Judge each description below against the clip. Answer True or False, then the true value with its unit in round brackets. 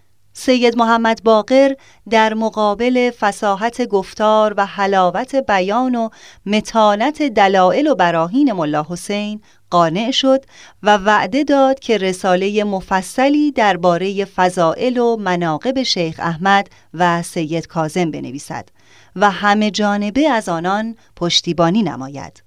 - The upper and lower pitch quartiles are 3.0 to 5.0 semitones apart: True (4.7 semitones)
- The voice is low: False (205 Hz)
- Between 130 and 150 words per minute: False (110 wpm)